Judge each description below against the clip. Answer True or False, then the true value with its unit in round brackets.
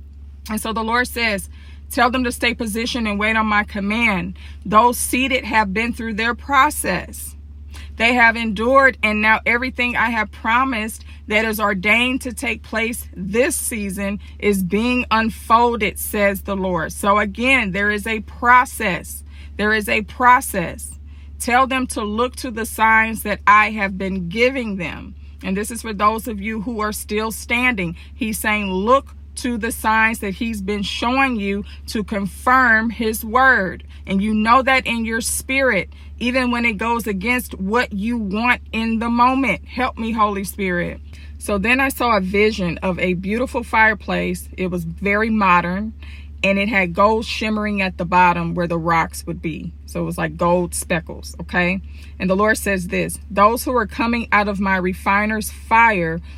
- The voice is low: False (215 Hz)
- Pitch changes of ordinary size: True (4.3 semitones)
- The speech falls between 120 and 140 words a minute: False (175 wpm)